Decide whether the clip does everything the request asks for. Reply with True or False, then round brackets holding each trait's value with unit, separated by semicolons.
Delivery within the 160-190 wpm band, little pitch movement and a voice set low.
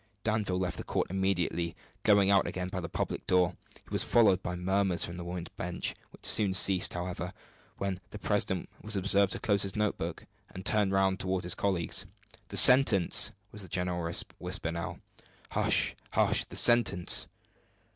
True (175 wpm; 2.0 semitones; 95 Hz)